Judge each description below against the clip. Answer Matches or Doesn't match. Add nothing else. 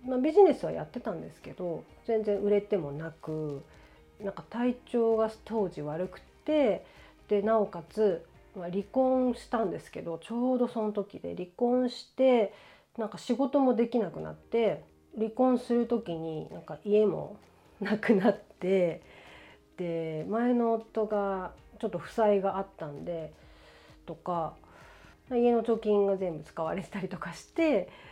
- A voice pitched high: Matches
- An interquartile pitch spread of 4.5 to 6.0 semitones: Matches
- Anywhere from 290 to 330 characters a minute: Doesn't match